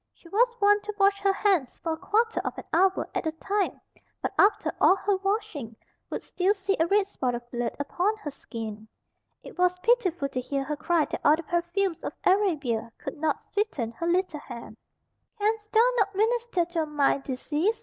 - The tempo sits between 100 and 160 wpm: No, average, 200 wpm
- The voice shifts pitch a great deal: Yes, wide, 5.8 semitones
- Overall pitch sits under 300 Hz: No, very high, 360 Hz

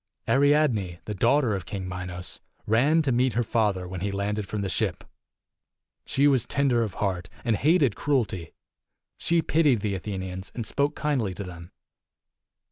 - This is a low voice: Yes, low, 105 Hz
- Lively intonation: Yes, wide, 6.6 semitones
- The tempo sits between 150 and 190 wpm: Yes, average, 170 wpm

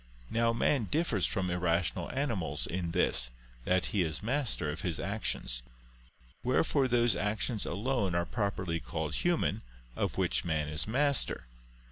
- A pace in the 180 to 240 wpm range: No, average, 140 wpm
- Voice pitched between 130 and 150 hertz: No, very low, 95 Hz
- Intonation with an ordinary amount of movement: No, wide, 6.1 semitones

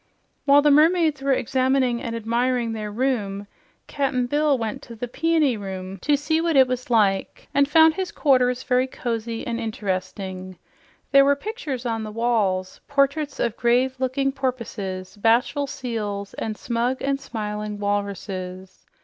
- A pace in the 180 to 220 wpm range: No, average, 155 wpm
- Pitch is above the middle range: Yes, high, 245 Hz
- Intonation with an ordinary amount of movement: Yes, average, 4.7 semitones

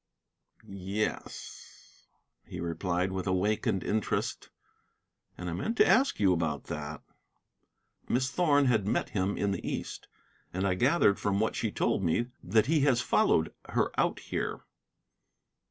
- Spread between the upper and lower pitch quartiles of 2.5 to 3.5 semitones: No, average, 4.6 semitones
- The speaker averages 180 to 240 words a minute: No, average, 140 wpm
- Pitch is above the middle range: No, low, 100 Hz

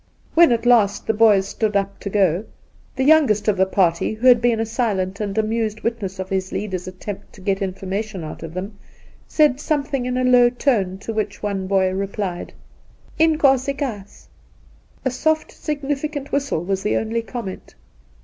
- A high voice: Yes, high, 215 Hz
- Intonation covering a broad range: No, average, 4.6 semitones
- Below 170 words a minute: No, average, 180 wpm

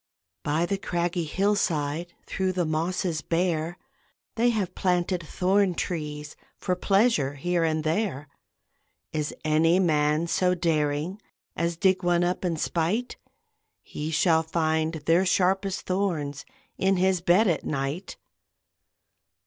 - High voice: No, medium, 170 Hz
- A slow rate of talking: Yes, slow, 125 wpm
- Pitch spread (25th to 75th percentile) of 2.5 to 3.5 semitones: Yes, average, 3.0 semitones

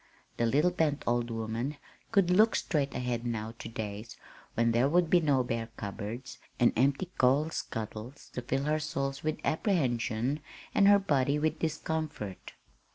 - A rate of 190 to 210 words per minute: No, average, 160 wpm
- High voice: No, low, 135 Hz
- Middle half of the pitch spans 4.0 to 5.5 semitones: Yes, average, 5.0 semitones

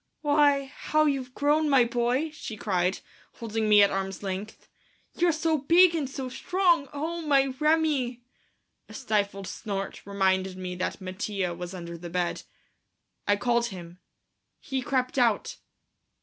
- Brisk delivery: No, average, 145 wpm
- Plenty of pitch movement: Yes, wide, 7.1 semitones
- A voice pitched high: Yes, high, 240 Hz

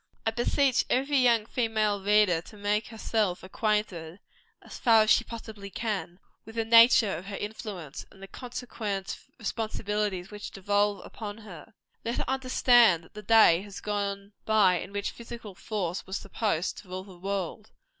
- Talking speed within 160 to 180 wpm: Yes, average, 165 wpm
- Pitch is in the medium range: No, high, 210 Hz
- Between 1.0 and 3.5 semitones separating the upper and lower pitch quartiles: Yes, narrow, 2.5 semitones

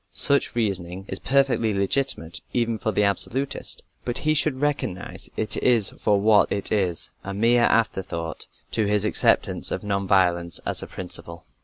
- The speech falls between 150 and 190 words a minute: Yes, average, 155 wpm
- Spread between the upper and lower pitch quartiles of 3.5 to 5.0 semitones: Yes, average, 4.0 semitones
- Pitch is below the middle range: Yes, low, 105 Hz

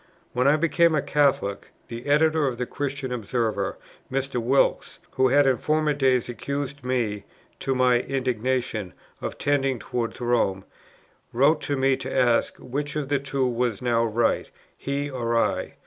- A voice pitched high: No, low, 130 Hz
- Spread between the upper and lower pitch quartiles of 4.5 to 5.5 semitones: No, average, 2.8 semitones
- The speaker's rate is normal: Yes, average, 160 wpm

